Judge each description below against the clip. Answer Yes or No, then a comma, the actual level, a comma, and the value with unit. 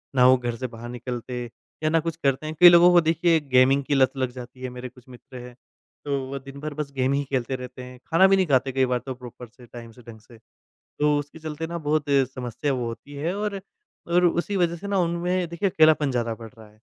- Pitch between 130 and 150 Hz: Yes, low, 135 Hz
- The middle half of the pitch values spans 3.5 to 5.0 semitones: Yes, average, 4.6 semitones